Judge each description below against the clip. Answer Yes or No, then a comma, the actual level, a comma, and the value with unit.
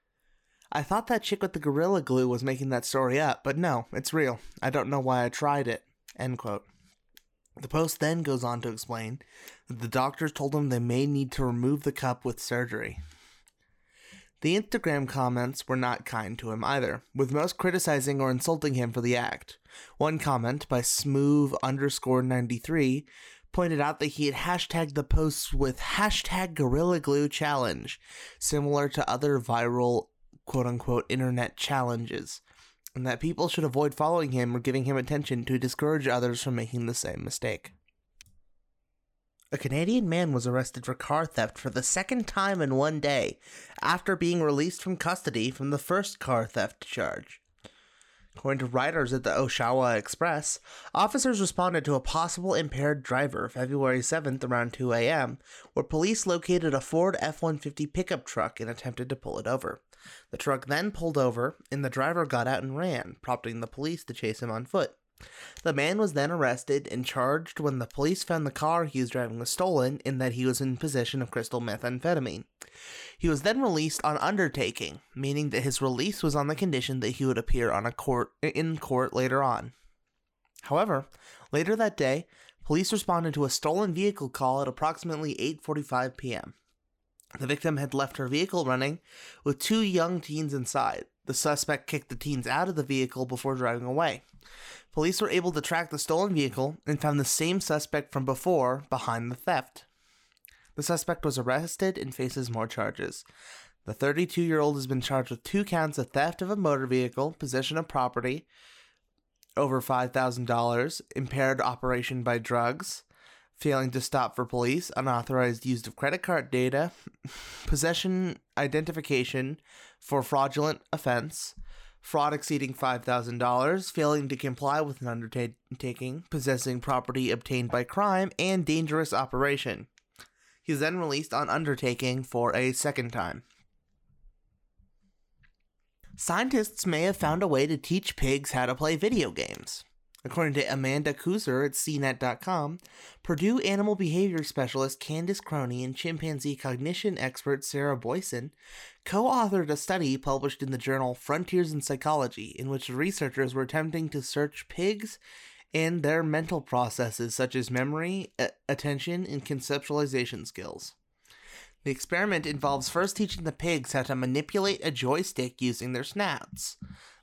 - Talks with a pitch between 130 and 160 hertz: Yes, medium, 140 Hz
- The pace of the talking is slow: No, average, 165 wpm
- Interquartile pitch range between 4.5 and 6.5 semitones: No, average, 3.9 semitones